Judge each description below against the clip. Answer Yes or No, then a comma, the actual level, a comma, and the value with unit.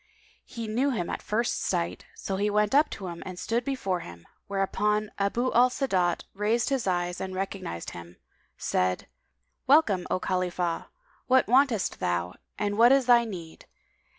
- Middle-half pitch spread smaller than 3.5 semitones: No, average, 5.1 semitones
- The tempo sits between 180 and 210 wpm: No, average, 160 wpm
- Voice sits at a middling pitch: No, high, 200 Hz